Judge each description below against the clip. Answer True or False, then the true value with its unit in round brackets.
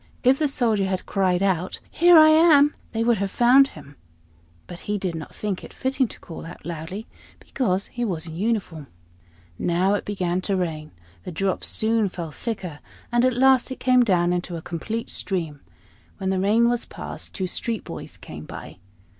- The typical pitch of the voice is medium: False (195 Hz)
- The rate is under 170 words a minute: False (190 wpm)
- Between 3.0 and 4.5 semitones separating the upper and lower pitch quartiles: False (5.3 semitones)